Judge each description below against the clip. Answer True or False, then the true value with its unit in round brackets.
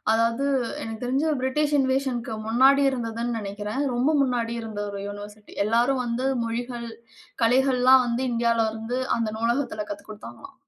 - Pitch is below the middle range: False (235 Hz)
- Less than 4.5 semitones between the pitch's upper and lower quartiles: True (2.6 semitones)